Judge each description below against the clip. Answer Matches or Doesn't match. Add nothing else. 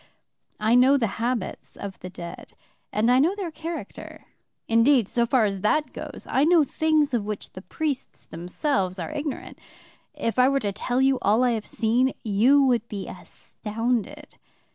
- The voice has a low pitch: Doesn't match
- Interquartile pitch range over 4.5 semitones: Matches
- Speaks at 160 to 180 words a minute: Matches